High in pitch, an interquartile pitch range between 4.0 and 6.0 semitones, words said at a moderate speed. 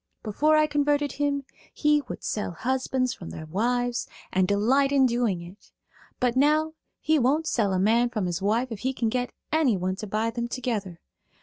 Yes: high, 245 Hz; average, 5.3 semitones; average, 185 wpm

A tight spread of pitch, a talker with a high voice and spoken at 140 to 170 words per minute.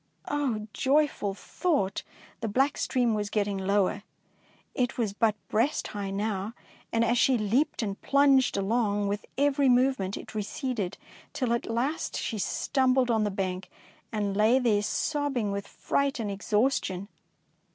No: average, 4.4 semitones; high, 225 Hz; average, 155 wpm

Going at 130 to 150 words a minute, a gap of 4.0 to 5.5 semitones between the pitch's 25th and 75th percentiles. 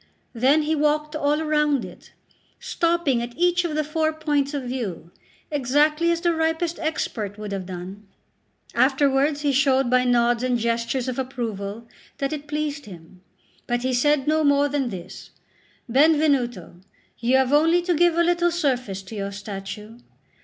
No: average, 160 wpm; average, 4.6 semitones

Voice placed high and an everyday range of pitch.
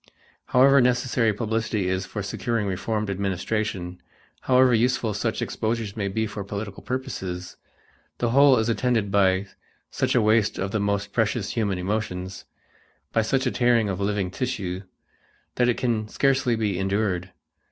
No: low, 110 Hz; average, 3.4 semitones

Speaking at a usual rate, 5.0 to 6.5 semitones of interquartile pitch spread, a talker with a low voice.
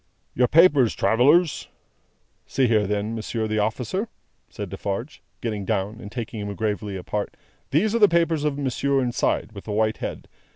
Yes: average, 165 wpm; average, 5.3 semitones; low, 115 Hz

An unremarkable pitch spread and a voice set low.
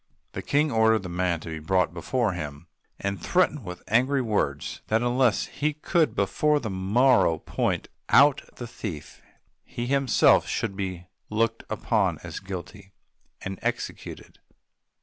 No: wide, 6.0 semitones; low, 110 Hz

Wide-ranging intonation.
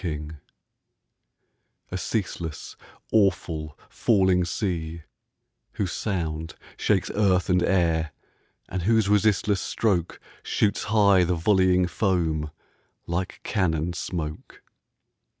No: average, 3.5 semitones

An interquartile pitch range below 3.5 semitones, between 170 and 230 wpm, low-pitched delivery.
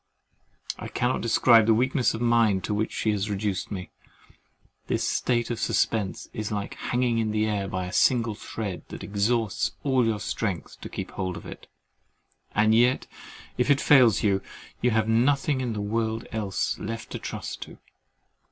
Yes: narrow, 2.6 semitones; average, 175 wpm; low, 110 Hz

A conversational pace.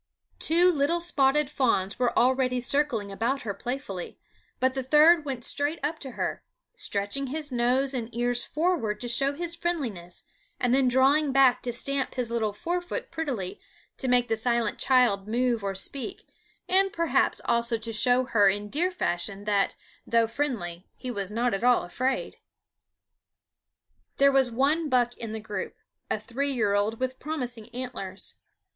Yes: average, 165 wpm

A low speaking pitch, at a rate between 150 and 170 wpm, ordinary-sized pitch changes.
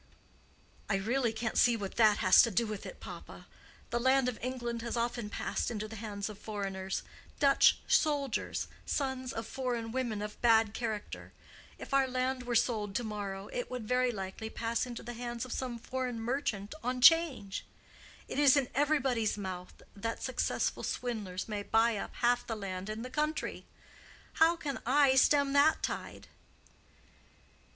No: high, 235 Hz; average, 160 wpm; average, 3.4 semitones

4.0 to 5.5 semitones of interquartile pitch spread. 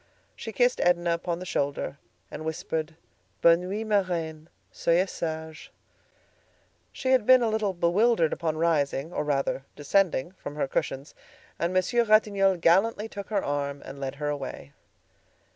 Yes: average, 4.8 semitones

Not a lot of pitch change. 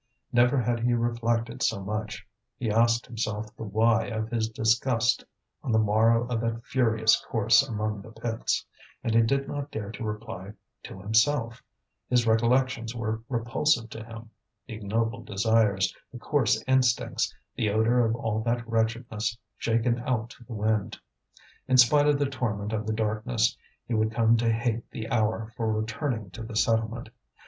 Yes: narrow, 1.5 semitones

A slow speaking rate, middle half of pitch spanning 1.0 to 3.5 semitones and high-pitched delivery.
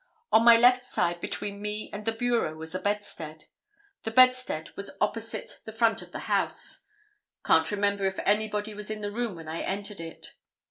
No: average, 185 wpm; average, 2.9 semitones; high, 210 Hz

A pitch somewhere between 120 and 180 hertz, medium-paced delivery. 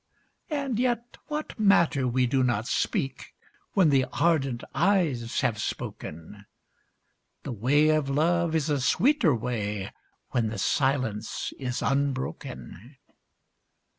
No: low, 135 Hz; slow, 115 wpm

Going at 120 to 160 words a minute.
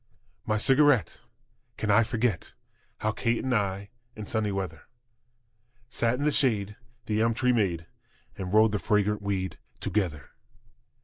Yes: average, 140 wpm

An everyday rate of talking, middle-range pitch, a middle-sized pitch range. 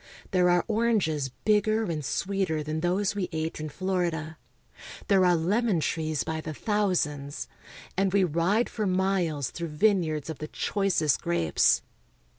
Yes: average, 150 wpm; medium, 175 Hz; average, 4.0 semitones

